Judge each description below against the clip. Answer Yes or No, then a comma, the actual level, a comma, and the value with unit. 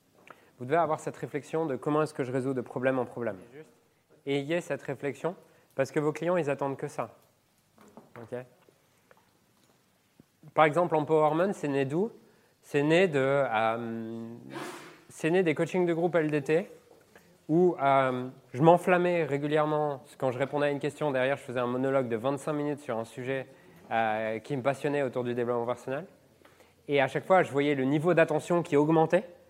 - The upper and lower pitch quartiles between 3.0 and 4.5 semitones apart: Yes, average, 3.5 semitones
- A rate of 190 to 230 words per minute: No, average, 175 wpm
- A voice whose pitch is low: No, medium, 145 Hz